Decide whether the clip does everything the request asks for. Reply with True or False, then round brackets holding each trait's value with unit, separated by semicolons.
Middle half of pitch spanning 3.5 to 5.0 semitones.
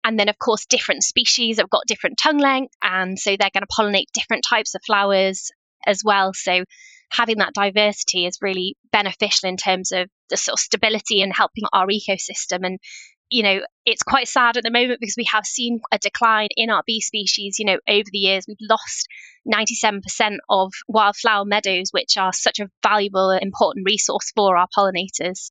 False (3.0 semitones)